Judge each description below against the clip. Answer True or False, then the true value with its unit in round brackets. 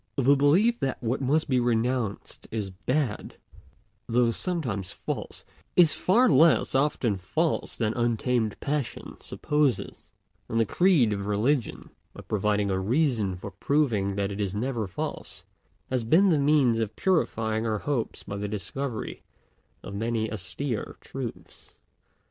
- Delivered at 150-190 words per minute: False (140 wpm)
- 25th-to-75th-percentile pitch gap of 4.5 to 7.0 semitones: True (5.3 semitones)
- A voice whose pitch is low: True (120 Hz)